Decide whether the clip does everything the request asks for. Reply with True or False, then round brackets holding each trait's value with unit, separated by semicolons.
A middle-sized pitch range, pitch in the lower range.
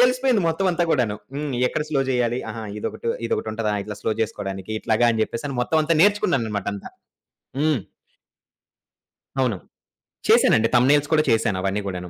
False (6.0 semitones; 120 Hz)